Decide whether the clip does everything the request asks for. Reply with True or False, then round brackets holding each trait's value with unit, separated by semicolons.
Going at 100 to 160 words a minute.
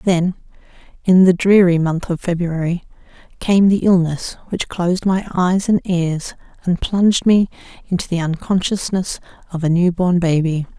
True (150 wpm)